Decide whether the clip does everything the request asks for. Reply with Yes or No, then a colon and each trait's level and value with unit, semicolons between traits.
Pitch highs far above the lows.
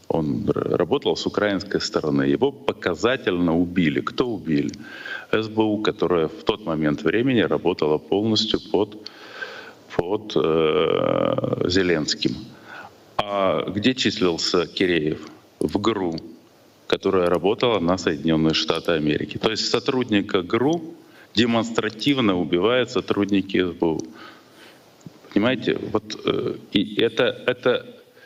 Yes: wide, 5.8 semitones